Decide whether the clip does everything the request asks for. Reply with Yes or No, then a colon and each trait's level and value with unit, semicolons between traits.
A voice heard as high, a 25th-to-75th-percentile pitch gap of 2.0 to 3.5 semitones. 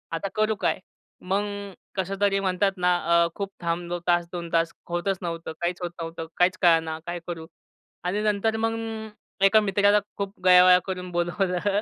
No: medium, 180 Hz; narrow, 2.5 semitones